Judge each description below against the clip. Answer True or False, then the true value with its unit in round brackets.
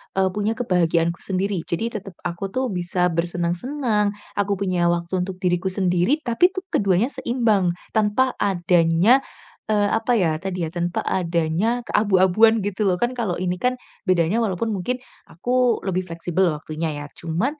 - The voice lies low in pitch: False (190 Hz)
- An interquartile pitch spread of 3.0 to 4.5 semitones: True (4.2 semitones)